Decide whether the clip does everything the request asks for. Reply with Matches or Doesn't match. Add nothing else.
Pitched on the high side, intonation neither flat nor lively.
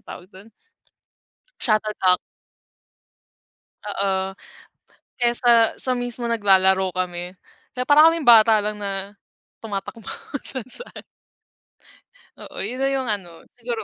Matches